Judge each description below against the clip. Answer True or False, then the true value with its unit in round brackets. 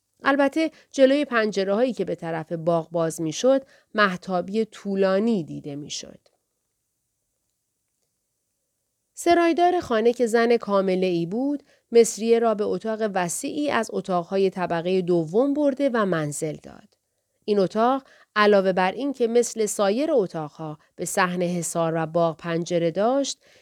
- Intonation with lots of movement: True (6.1 semitones)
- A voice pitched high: True (205 Hz)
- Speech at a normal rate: True (130 wpm)